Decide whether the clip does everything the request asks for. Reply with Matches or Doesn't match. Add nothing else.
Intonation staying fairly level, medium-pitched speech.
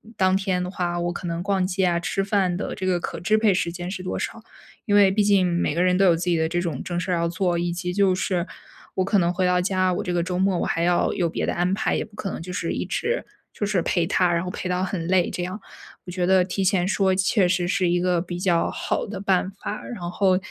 Matches